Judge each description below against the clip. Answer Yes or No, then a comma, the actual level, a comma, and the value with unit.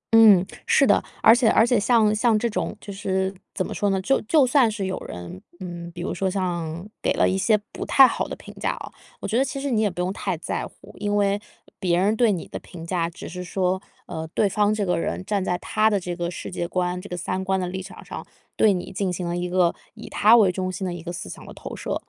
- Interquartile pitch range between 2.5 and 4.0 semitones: Yes, average, 3.2 semitones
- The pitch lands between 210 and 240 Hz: No, high, 190 Hz